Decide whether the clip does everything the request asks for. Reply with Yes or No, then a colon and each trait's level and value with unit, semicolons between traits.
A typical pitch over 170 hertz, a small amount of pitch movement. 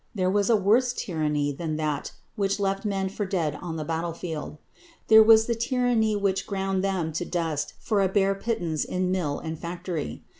No: high, 190 Hz; average, 4.0 semitones